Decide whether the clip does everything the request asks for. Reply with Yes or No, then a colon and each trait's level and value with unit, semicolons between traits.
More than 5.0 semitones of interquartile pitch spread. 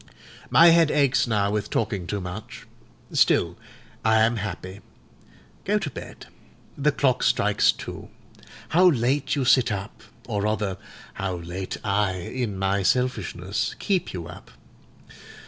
Yes: wide, 5.6 semitones